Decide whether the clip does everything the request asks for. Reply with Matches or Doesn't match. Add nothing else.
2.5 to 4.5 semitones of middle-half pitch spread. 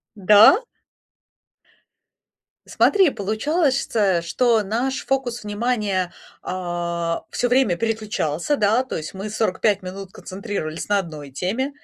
Doesn't match